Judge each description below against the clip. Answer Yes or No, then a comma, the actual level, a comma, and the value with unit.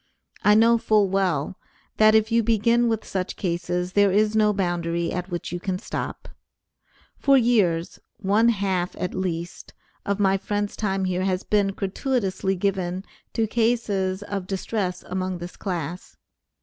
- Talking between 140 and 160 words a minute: Yes, average, 150 wpm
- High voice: Yes, high, 195 Hz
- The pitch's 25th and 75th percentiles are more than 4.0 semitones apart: No, average, 2.8 semitones